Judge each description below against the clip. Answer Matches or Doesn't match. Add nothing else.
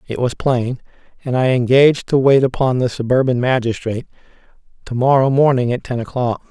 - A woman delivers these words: Doesn't match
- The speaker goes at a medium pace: Matches